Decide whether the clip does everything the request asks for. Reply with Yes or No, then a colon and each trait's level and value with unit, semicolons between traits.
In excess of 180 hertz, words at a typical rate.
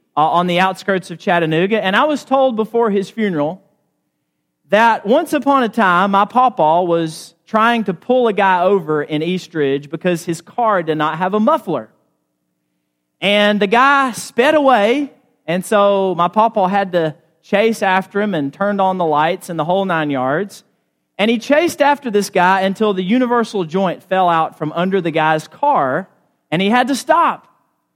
Yes: high, 190 Hz; average, 180 wpm